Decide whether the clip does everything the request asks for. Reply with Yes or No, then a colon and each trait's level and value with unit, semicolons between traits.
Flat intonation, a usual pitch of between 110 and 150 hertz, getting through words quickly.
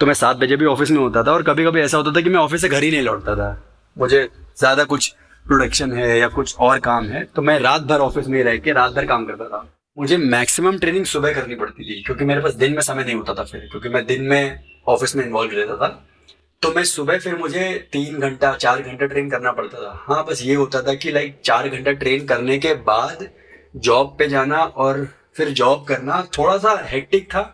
No: average, 3.3 semitones; medium, 140 Hz; fast, 240 wpm